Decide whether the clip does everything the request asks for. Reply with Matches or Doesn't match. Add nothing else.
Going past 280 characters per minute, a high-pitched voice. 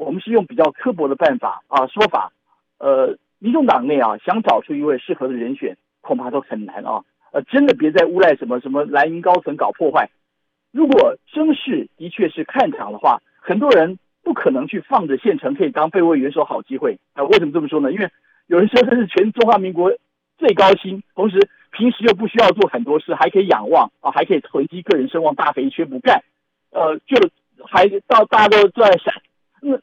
Matches